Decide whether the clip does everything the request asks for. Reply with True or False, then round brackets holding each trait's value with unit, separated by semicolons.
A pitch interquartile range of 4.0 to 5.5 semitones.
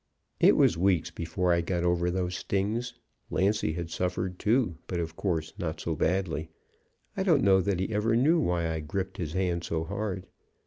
False (2.9 semitones)